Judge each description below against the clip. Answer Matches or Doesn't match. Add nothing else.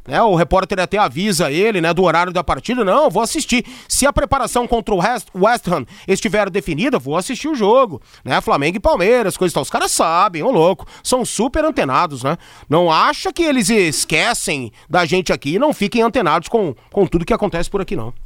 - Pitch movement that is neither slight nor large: Doesn't match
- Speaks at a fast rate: Matches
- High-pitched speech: Matches